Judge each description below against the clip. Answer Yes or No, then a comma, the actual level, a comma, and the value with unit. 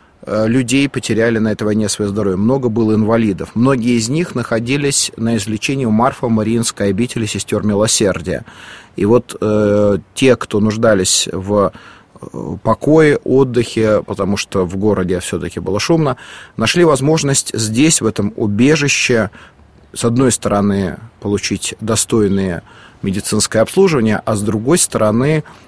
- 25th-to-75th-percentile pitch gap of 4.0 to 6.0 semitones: No, average, 3.5 semitones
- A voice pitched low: Yes, low, 110 Hz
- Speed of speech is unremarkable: Yes, average, 130 wpm